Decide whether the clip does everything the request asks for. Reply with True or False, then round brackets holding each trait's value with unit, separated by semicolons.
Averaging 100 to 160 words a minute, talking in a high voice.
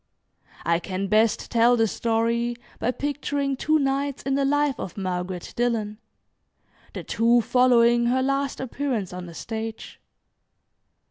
True (135 wpm; 235 Hz)